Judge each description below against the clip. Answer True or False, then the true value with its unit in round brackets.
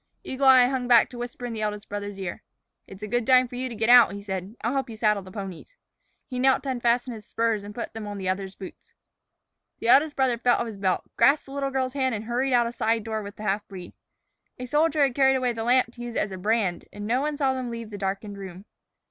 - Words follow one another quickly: True (270 wpm)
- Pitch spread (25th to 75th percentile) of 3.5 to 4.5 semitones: True (3.8 semitones)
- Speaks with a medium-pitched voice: False (235 Hz)